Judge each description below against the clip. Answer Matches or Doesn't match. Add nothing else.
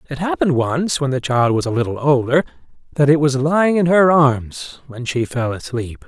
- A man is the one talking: Matches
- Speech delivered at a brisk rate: Matches